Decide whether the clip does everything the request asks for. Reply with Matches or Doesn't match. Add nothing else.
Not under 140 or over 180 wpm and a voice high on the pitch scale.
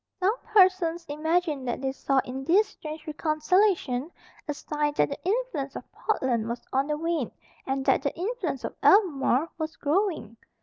Matches